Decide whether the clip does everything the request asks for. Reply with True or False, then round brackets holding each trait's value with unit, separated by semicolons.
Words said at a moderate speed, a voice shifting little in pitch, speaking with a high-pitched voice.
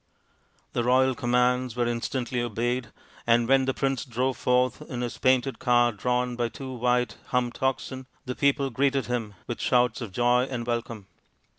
False (165 wpm; 1.4 semitones; 125 Hz)